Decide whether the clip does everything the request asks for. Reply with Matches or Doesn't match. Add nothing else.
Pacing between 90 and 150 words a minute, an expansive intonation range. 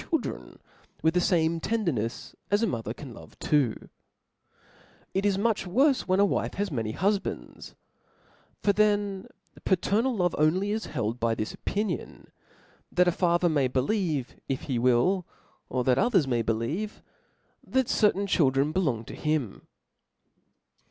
Matches